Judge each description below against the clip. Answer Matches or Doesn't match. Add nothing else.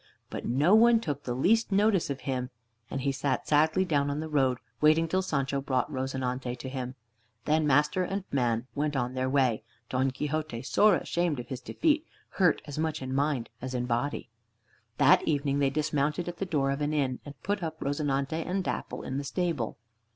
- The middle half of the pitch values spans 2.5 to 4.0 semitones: Matches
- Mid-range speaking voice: Matches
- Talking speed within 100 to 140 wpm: Doesn't match